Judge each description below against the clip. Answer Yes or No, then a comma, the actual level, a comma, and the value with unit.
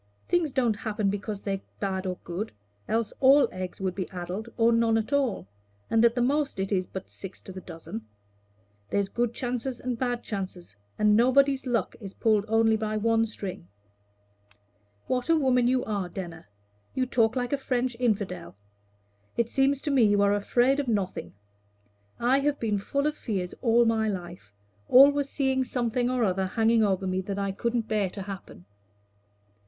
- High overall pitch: Yes, high, 225 Hz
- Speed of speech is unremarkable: Yes, average, 180 wpm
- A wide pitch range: No, average, 4.3 semitones